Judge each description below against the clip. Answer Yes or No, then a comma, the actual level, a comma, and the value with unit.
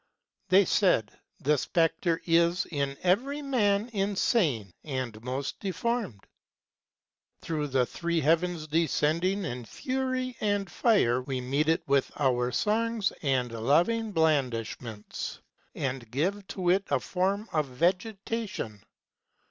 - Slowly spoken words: Yes, slow, 120 wpm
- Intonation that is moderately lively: No, wide, 7.2 semitones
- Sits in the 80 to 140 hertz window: No, medium, 165 Hz